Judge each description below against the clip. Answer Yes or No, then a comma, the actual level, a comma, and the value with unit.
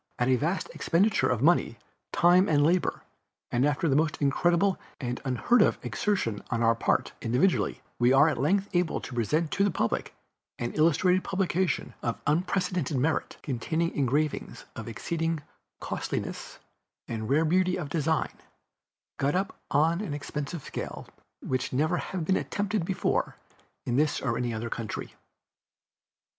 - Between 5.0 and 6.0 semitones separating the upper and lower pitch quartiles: Yes, wide, 5.5 semitones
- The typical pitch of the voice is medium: Yes, medium, 155 Hz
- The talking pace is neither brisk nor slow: Yes, average, 150 wpm